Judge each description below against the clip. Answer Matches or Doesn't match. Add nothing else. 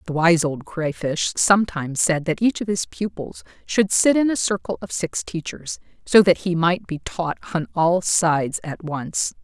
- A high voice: Doesn't match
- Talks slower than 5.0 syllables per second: Matches